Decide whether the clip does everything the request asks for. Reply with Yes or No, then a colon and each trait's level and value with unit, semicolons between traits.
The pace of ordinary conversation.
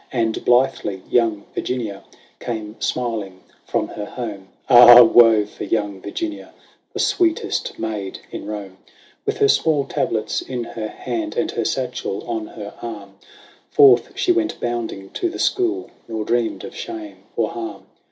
Yes: average, 150 wpm